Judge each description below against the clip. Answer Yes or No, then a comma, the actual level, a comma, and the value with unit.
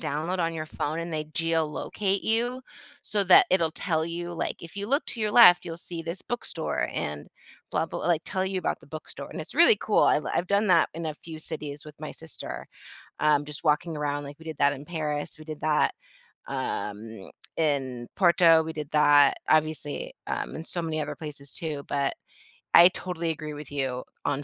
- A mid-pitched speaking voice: Yes, medium, 160 Hz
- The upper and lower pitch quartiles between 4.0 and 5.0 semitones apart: No, average, 2.8 semitones